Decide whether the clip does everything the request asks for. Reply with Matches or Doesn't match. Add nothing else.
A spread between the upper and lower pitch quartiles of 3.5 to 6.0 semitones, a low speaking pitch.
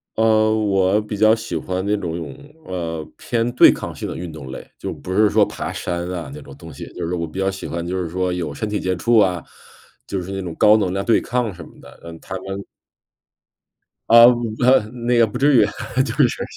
Matches